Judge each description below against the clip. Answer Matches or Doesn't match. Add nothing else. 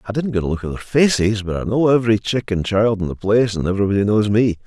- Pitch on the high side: Doesn't match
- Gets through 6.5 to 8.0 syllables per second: Matches